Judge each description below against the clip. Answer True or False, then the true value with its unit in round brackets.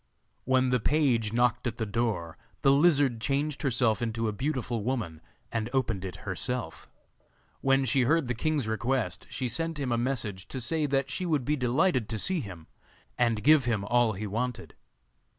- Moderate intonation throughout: True (3.7 semitones)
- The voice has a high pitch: False (125 Hz)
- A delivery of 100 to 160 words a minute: False (180 wpm)